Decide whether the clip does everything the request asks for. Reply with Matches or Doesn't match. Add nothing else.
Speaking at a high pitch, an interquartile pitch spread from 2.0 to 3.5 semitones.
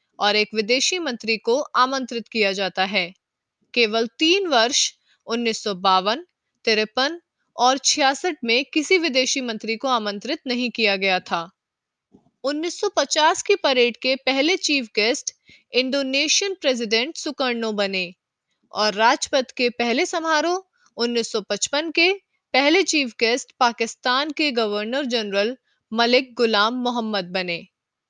Doesn't match